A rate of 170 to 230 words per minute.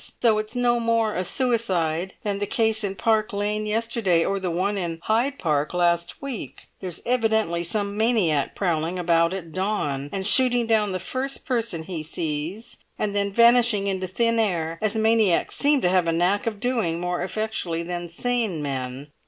Yes: average, 175 wpm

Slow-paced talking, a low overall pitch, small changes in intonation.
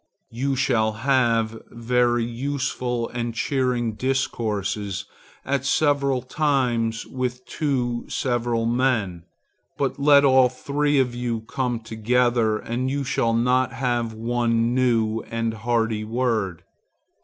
Yes: slow, 115 wpm; low, 120 Hz; narrow, 2.3 semitones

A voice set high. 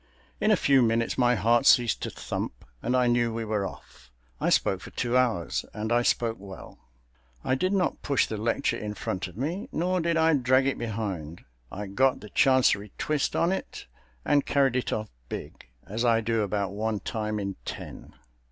No: low, 115 Hz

